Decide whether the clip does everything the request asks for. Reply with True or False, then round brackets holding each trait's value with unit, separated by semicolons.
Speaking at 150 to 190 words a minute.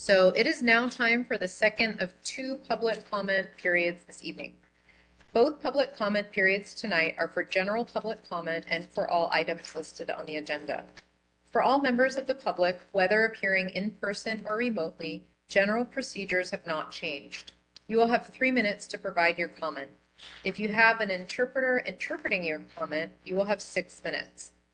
True (175 wpm)